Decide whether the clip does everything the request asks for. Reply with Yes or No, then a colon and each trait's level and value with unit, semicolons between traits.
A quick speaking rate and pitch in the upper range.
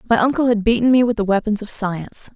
Yes: fast, 255 wpm; high, 220 Hz